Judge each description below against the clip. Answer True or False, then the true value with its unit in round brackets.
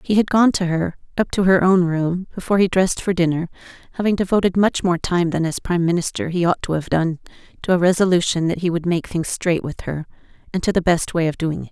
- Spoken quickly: True (245 wpm)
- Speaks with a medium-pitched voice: True (175 Hz)